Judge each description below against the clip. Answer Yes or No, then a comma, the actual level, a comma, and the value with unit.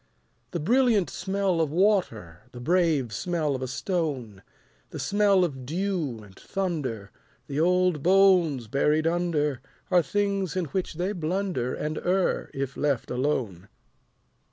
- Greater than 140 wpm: No, slow, 135 wpm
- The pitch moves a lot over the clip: Yes, wide, 5.9 semitones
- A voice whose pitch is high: No, medium, 160 Hz